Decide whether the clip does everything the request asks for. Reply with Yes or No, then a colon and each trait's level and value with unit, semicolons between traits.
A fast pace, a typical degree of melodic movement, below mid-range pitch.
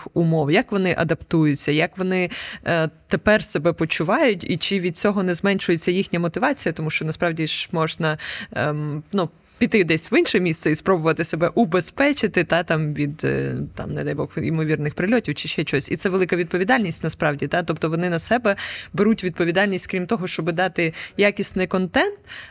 No: fast, 175 wpm; average, 3.3 semitones; medium, 175 Hz